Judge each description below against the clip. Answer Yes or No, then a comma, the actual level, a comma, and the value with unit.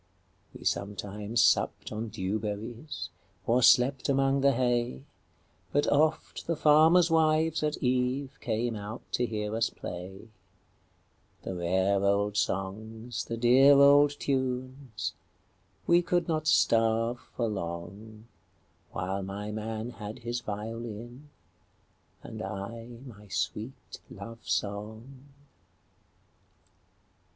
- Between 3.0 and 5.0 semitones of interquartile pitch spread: Yes, average, 4.3 semitones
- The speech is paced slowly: Yes, slow, 95 wpm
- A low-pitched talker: Yes, low, 115 Hz